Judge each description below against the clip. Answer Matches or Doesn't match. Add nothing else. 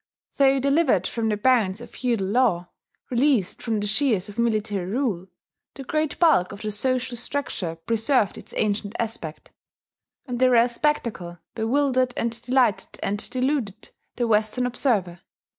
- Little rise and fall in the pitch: Doesn't match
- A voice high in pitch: Matches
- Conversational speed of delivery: Matches